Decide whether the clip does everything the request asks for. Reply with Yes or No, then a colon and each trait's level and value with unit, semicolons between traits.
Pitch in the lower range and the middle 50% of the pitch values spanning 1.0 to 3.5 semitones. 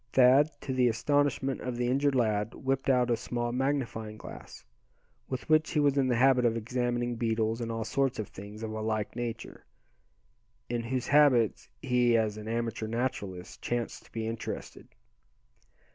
Yes: low, 120 Hz; average, 2.8 semitones